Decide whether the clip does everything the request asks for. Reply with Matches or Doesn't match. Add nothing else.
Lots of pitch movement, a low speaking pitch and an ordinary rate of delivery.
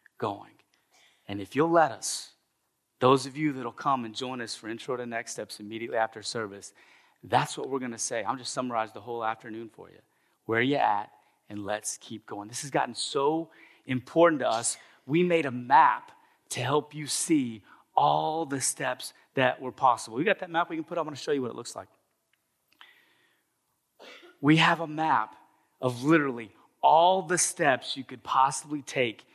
Matches